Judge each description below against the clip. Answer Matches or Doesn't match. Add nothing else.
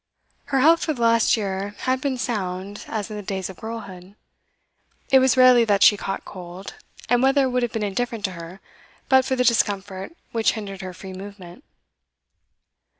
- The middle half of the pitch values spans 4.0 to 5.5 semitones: Matches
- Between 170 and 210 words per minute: Matches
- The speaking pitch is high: Matches